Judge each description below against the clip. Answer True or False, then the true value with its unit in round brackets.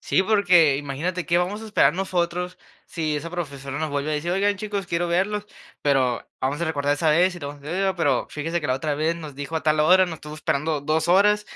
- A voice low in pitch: False (165 Hz)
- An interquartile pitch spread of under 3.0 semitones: False (3.7 semitones)